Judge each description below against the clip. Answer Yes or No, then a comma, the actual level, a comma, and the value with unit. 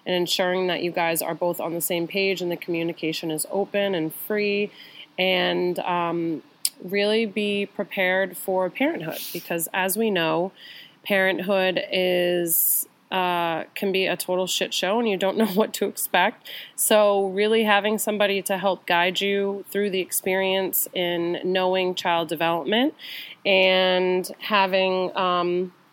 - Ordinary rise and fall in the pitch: No, narrow, 2.2 semitones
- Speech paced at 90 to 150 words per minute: Yes, average, 145 wpm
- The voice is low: No, medium, 185 Hz